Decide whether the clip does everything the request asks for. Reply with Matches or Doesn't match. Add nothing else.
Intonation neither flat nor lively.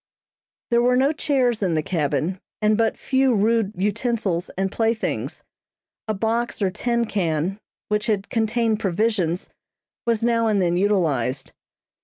Matches